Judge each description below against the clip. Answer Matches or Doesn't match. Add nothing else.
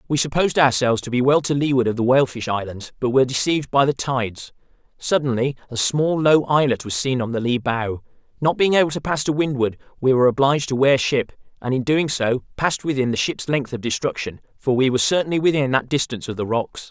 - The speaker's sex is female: Doesn't match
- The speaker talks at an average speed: Doesn't match